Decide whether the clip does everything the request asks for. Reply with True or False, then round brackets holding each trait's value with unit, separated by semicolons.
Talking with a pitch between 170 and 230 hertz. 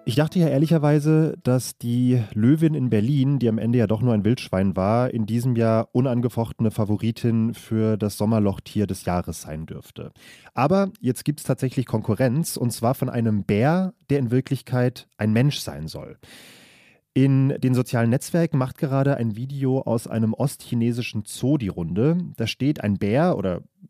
False (125 Hz)